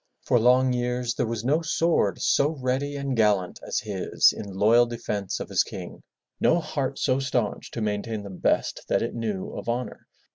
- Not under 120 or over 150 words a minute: No, average, 185 wpm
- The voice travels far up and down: No, average, 3.8 semitones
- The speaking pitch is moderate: No, low, 120 Hz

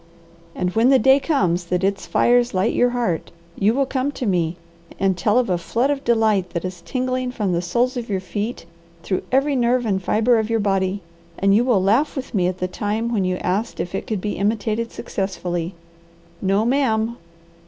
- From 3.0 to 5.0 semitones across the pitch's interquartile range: Yes, average, 4.6 semitones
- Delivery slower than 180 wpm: No, fast, 205 wpm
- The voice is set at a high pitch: Yes, high, 210 Hz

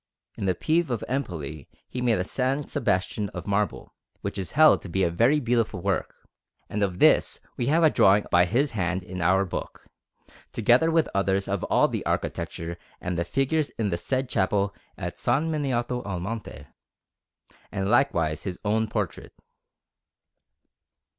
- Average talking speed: Yes, average, 165 wpm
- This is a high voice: No, low, 105 Hz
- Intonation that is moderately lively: No, wide, 5.9 semitones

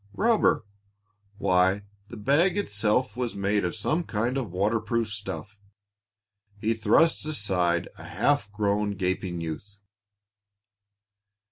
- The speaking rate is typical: No, slow, 110 wpm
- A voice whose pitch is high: No, low, 105 Hz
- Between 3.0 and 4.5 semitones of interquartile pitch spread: Yes, average, 3.6 semitones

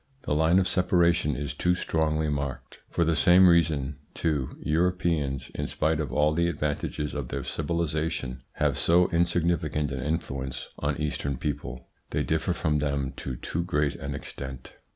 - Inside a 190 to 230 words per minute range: No, average, 160 wpm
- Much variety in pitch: No, average, 3.1 semitones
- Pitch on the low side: Yes, very low, 75 Hz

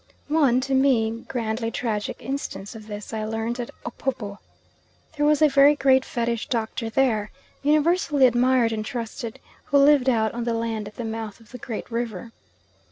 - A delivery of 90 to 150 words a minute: No, average, 170 wpm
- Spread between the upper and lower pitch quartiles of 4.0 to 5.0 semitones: No, average, 3.3 semitones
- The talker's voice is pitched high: Yes, high, 235 Hz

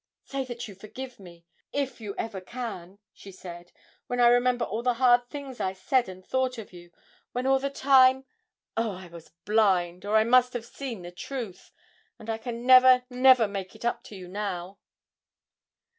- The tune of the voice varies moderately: Yes, average, 5.0 semitones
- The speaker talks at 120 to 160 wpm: No, average, 190 wpm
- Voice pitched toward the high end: Yes, high, 230 Hz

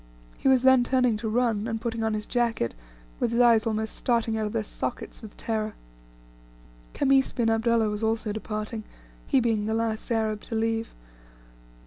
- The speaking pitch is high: Yes, high, 225 Hz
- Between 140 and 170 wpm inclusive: No, average, 180 wpm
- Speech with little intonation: Yes, narrow, 1.5 semitones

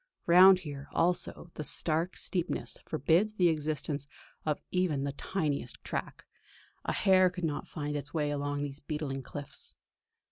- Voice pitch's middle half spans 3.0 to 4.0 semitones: Yes, average, 3.7 semitones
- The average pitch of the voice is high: No, medium, 155 Hz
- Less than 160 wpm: Yes, average, 145 wpm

